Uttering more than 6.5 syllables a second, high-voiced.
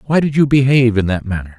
No: 7.0 syllables/s; low, 120 Hz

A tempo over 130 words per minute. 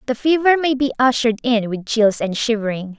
Yes: average, 200 wpm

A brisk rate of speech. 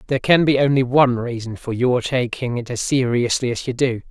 Yes: fast, 220 wpm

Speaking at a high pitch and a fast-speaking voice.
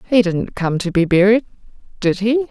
No: high, 205 Hz; average, 170 wpm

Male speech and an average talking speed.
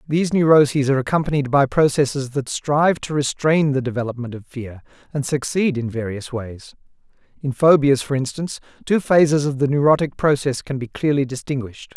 Yes: male; average, 165 wpm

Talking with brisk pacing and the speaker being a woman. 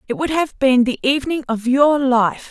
Yes: fast, 215 wpm; female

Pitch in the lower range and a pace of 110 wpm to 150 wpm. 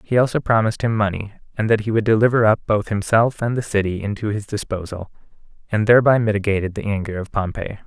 No: low, 105 Hz; average, 200 wpm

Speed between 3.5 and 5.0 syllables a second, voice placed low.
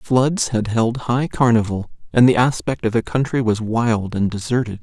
Yes: 4.6 syllables/s; low, 115 Hz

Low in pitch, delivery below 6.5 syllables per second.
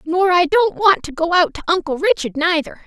No: very high, 345 Hz; 5.3 syllables/s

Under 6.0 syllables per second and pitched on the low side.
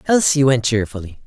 Yes: 5.5 syllables/s; low, 130 Hz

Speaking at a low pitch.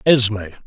Yes: low, 110 Hz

